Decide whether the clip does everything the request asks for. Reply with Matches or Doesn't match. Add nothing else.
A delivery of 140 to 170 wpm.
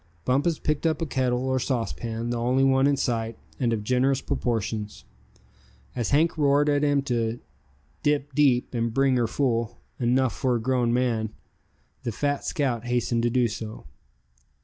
Matches